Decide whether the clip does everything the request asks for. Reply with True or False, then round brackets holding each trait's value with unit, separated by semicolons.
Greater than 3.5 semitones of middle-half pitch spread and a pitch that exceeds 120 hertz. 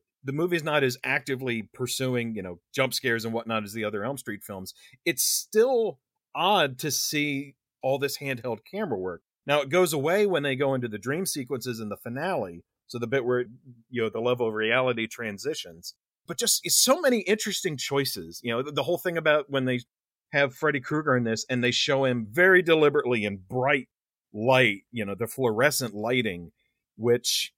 True (4.3 semitones; 130 Hz)